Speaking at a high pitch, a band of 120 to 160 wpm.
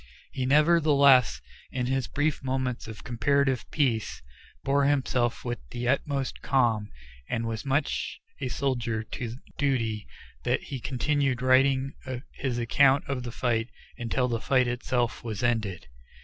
No: low, 125 Hz; average, 140 wpm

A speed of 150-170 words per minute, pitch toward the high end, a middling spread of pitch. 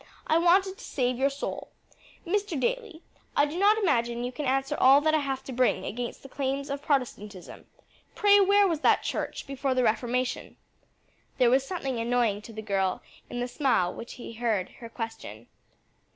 No: average, 185 wpm; very high, 265 Hz; average, 4.8 semitones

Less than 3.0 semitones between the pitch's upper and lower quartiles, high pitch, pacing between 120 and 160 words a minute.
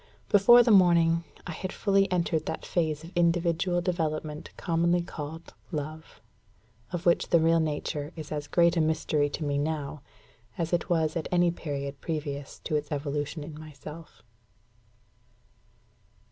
No: narrow, 2.4 semitones; medium, 160 Hz; average, 145 wpm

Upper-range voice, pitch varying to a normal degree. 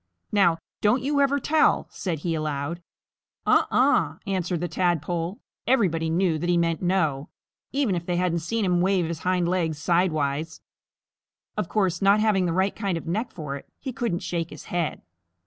No: medium, 175 Hz; average, 3.1 semitones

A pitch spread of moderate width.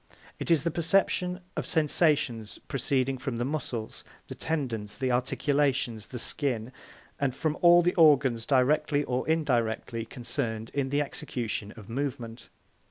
Yes: average, 4.2 semitones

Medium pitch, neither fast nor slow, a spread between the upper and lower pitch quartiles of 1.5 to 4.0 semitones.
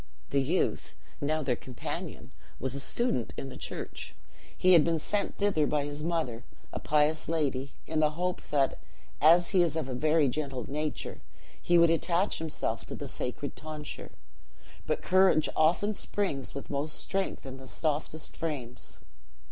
Yes: medium, 150 Hz; average, 165 wpm; average, 3.3 semitones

